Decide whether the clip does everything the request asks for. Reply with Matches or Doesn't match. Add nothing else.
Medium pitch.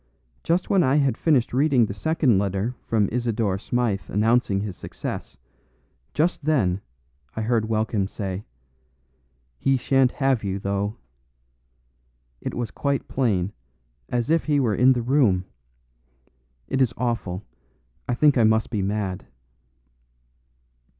Doesn't match